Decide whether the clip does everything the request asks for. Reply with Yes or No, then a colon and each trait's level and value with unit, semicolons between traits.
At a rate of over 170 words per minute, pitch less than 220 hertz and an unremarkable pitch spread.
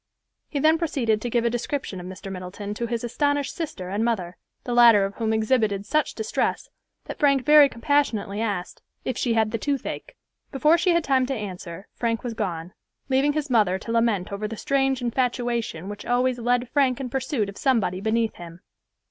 No: average, 190 wpm; high, 235 Hz; average, 4.6 semitones